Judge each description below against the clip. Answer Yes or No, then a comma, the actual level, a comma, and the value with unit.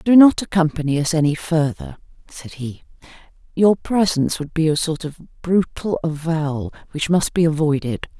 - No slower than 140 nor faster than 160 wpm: Yes, average, 155 wpm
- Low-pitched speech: No, medium, 160 Hz